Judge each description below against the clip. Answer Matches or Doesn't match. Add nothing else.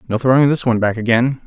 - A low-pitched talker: Matches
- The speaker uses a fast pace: Matches